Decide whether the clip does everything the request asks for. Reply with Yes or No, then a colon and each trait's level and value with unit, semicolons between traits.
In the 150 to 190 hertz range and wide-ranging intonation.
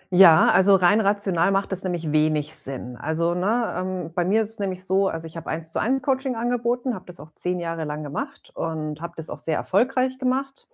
Yes: medium, 185 Hz; wide, 5.7 semitones